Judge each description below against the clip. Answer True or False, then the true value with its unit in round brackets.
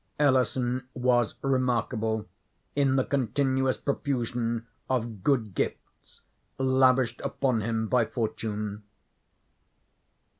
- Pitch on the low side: True (125 Hz)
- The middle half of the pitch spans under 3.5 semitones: True (2.8 semitones)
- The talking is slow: True (85 wpm)